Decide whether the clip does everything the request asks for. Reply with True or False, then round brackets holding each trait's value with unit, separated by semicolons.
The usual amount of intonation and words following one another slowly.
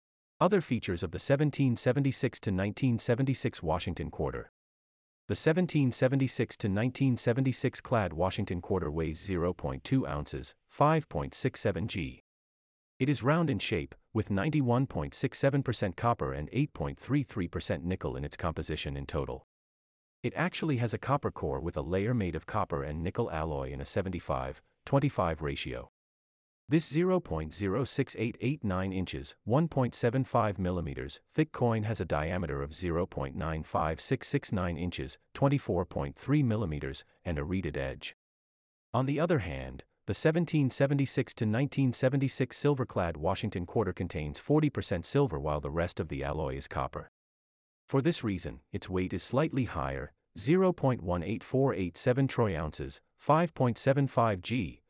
False (9.0 semitones; 115 wpm)